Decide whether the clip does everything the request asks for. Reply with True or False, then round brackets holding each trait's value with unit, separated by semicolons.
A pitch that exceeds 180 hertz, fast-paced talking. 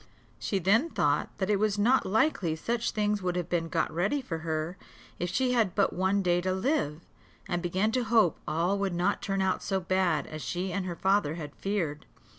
True (190 Hz; 210 wpm)